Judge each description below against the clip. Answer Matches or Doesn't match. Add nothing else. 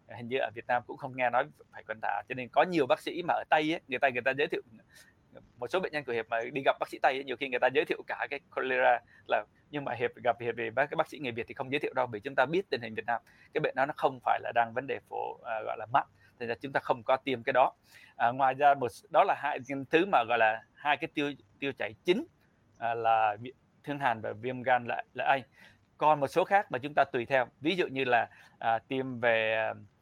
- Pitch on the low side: Matches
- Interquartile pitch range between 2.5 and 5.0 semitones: Matches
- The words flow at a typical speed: Doesn't match